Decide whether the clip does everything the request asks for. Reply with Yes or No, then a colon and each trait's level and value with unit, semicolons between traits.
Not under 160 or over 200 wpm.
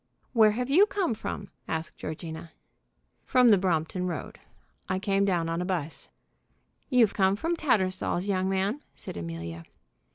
No: average, 150 wpm